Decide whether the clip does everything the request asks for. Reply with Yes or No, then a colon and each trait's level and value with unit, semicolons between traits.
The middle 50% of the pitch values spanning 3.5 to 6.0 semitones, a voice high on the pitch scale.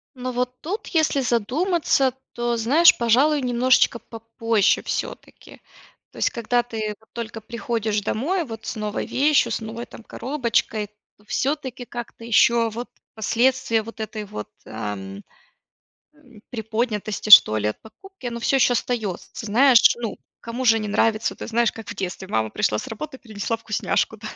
No: average, 2.8 semitones; high, 230 Hz